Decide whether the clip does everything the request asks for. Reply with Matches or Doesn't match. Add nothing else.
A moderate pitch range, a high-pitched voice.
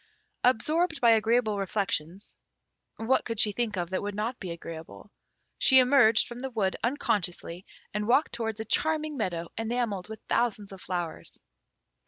Matches